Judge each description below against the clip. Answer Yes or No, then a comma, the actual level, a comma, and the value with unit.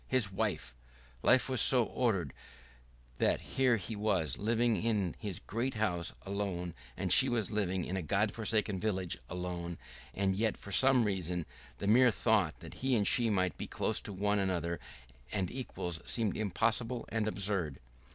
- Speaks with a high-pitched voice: No, low, 100 Hz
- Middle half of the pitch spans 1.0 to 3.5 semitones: No, average, 3.9 semitones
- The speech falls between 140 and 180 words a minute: Yes, average, 165 wpm